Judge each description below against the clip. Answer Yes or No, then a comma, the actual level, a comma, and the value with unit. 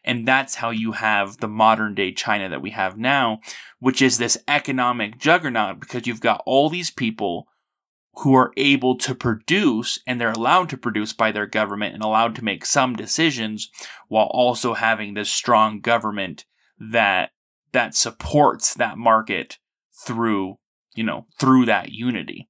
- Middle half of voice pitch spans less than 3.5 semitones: Yes, average, 3.0 semitones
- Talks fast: No, average, 160 wpm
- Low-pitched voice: Yes, low, 115 Hz